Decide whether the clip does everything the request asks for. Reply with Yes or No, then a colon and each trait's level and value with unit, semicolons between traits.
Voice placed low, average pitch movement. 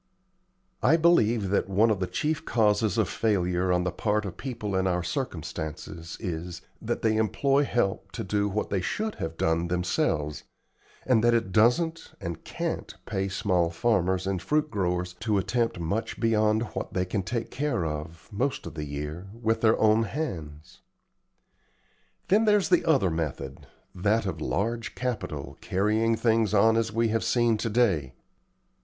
Yes: low, 105 Hz; average, 4.5 semitones